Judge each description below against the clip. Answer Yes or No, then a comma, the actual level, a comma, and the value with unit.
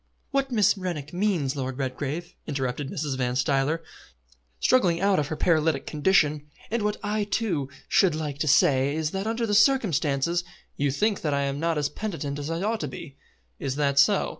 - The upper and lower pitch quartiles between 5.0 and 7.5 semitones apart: Yes, wide, 5.6 semitones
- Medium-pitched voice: Yes, medium, 155 Hz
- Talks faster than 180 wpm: Yes, average, 190 wpm